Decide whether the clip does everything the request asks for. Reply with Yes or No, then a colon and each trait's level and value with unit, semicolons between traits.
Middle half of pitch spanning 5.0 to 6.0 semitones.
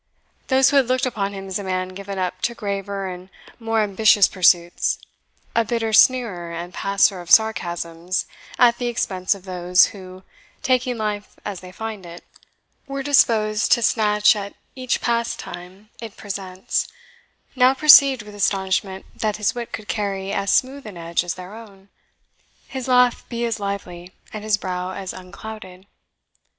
No: average, 3.7 semitones